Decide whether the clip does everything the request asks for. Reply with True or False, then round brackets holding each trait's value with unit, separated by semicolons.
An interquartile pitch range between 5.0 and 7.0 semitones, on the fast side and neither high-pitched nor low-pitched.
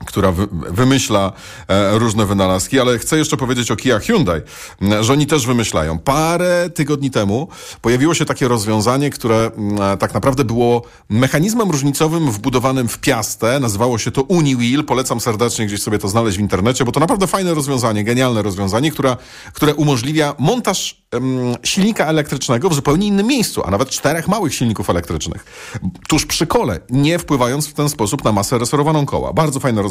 False (5.4 semitones; 165 wpm; 130 Hz)